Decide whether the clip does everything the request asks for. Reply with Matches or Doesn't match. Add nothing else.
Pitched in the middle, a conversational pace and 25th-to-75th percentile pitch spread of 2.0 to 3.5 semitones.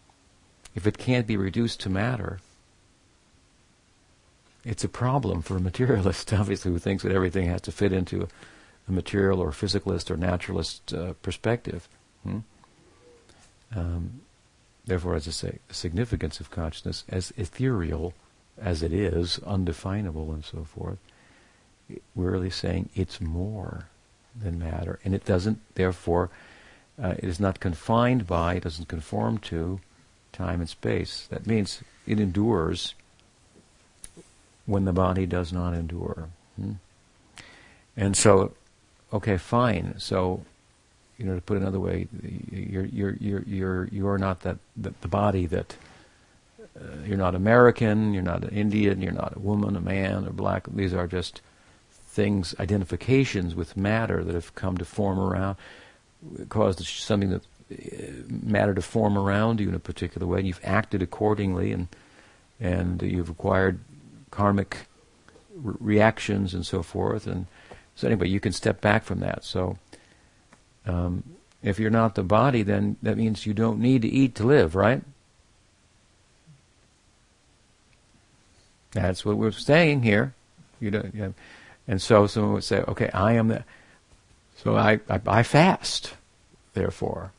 Doesn't match